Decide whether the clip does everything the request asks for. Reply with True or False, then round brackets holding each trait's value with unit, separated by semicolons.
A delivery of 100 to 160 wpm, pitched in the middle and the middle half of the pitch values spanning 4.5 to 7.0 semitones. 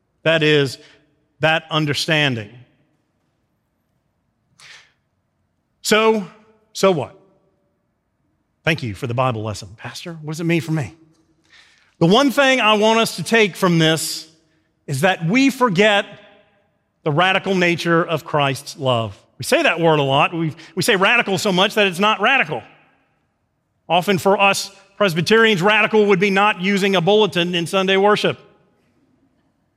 True (140 wpm; 175 Hz; 4.9 semitones)